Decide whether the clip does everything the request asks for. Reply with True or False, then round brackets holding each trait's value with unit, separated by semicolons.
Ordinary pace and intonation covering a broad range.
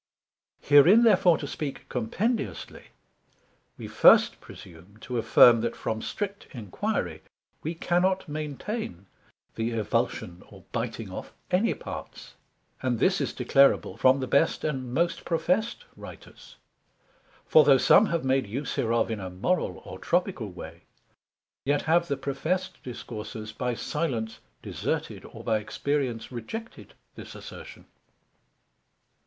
False (125 wpm; 7.1 semitones)